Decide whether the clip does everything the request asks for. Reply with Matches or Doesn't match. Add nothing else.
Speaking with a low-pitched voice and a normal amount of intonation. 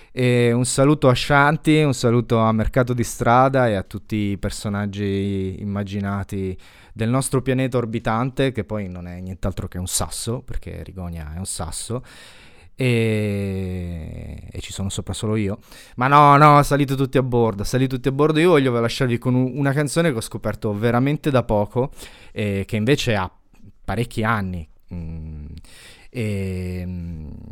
Matches